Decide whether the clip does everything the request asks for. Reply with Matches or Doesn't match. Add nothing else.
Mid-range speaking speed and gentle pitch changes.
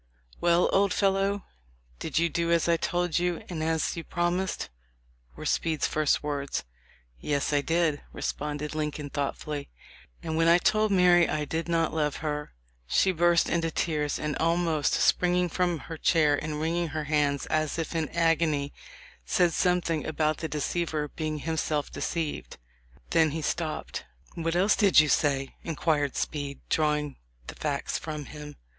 Matches